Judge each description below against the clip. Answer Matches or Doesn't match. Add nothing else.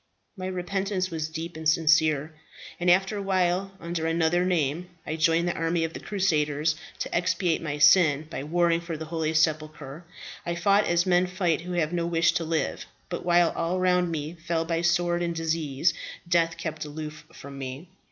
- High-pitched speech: Doesn't match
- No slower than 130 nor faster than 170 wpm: Doesn't match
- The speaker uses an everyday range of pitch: Doesn't match